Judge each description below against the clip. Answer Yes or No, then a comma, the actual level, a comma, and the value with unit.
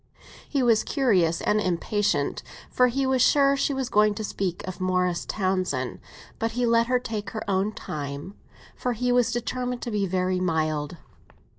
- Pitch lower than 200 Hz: No, high, 210 Hz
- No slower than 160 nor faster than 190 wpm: Yes, average, 170 wpm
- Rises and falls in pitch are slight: No, average, 5.2 semitones